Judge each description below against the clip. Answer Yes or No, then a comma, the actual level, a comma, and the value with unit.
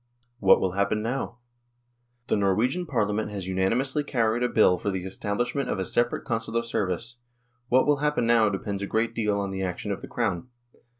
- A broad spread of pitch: No, average, 3.7 semitones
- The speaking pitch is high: No, low, 110 Hz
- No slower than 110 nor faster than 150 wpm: No, average, 195 wpm